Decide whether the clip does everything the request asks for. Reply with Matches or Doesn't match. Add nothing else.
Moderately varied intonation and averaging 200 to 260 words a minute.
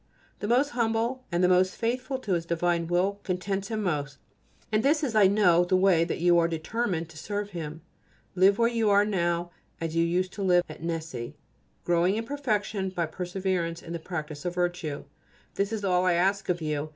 Matches